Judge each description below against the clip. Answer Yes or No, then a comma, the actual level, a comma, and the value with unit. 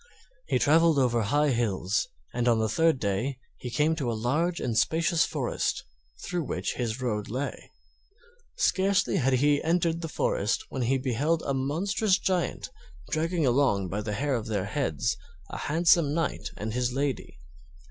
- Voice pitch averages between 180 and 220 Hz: No, low, 135 Hz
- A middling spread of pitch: No, wide, 5.9 semitones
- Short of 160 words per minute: No, average, 165 wpm